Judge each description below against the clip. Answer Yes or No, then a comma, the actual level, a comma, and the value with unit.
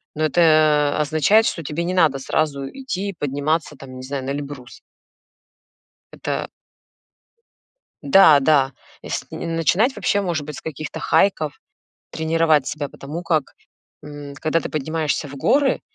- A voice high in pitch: No, medium, 155 Hz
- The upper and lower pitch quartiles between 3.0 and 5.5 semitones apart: No, narrow, 2.6 semitones